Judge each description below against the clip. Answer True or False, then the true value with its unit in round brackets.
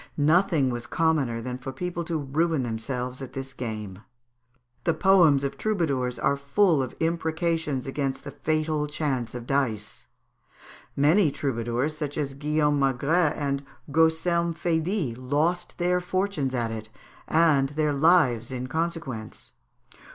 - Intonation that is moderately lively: True (4.2 semitones)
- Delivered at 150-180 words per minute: False (135 wpm)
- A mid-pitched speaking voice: True (145 Hz)